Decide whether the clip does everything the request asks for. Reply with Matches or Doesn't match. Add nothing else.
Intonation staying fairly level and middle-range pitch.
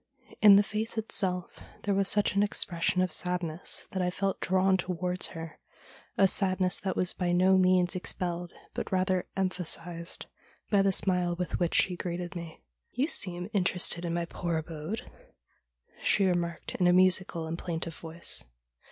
Matches